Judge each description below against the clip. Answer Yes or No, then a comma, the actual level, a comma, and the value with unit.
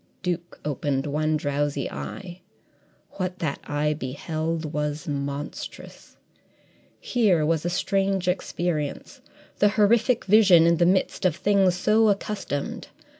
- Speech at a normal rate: No, slow, 120 wpm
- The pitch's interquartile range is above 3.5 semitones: Yes, average, 4.5 semitones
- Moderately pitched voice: Yes, medium, 170 Hz